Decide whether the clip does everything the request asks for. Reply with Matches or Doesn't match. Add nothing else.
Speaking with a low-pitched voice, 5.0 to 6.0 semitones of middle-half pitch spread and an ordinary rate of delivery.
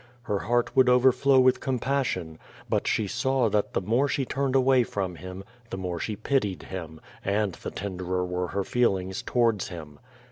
Matches